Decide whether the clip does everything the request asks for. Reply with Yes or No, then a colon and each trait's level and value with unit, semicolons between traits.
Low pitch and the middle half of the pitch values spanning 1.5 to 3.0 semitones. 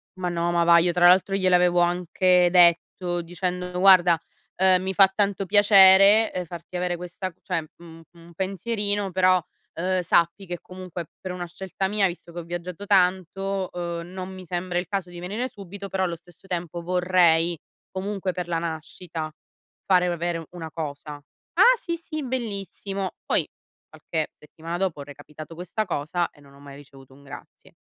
No: medium, 180 Hz; narrow, 2.0 semitones